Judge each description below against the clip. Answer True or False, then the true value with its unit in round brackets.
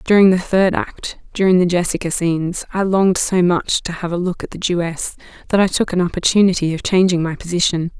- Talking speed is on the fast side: True (210 wpm)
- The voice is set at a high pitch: False (180 Hz)